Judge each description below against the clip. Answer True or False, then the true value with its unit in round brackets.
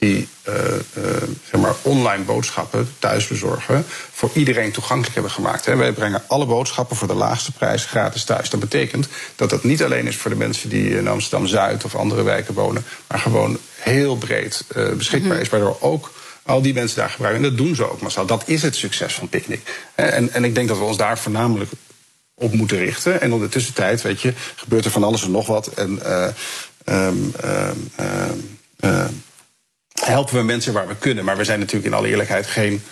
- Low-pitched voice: True (115 Hz)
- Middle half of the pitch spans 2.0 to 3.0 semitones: False (3.4 semitones)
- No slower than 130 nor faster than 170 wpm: False (190 wpm)